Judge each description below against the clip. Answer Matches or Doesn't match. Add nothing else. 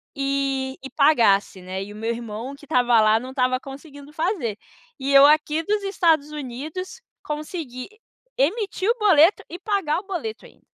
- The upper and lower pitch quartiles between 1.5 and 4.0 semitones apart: Doesn't match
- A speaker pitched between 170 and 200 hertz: Doesn't match